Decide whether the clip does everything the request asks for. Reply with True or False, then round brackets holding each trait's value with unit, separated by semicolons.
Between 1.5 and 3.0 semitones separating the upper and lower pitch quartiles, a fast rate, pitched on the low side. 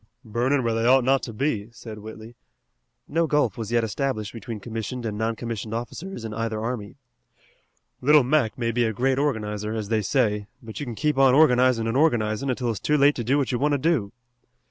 False (3.5 semitones; 210 wpm; 120 Hz)